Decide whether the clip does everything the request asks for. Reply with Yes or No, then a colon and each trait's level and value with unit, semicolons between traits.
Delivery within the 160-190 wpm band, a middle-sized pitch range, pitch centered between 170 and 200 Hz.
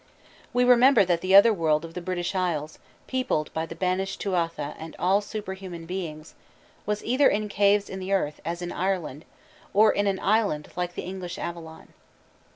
Yes: average, 170 wpm; average, 3.3 semitones; medium, 185 Hz